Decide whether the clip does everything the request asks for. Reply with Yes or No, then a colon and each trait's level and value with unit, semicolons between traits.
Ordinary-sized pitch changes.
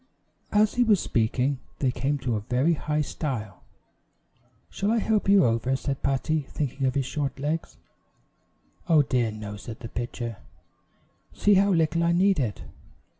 No: wide, 5.7 semitones